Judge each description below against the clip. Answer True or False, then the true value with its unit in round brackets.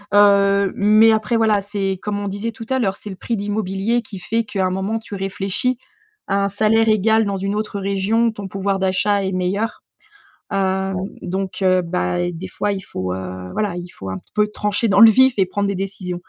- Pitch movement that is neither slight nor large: False (2.1 semitones)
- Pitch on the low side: False (200 Hz)